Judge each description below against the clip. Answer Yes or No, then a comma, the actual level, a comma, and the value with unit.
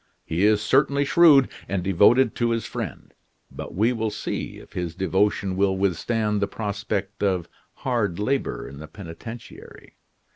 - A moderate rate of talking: Yes, average, 150 wpm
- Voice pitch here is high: No, low, 105 Hz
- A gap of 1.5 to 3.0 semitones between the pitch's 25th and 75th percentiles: No, average, 3.6 semitones